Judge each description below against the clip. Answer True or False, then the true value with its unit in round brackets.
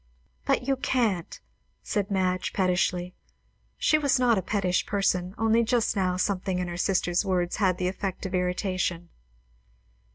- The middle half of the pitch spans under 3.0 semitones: True (2.5 semitones)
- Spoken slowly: False (150 wpm)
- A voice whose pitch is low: False (185 Hz)